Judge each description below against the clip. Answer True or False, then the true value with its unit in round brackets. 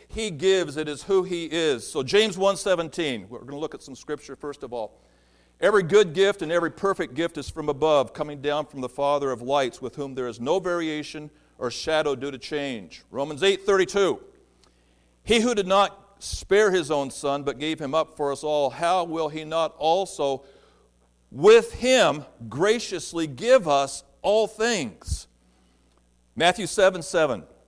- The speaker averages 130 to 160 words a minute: False (180 wpm)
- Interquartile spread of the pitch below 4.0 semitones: False (5.5 semitones)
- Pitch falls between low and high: True (155 Hz)